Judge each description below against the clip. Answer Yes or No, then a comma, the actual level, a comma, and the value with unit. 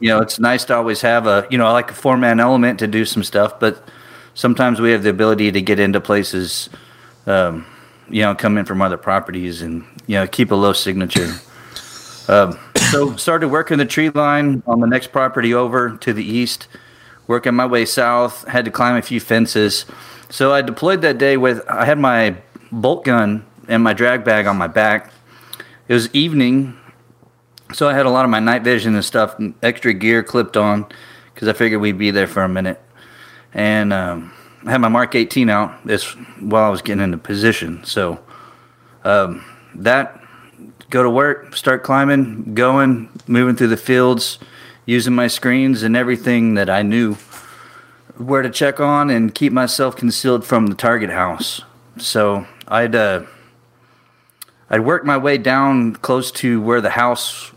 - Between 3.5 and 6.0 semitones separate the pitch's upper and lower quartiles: No, average, 2.9 semitones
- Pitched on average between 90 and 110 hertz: No, low, 120 Hz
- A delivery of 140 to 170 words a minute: No, average, 185 wpm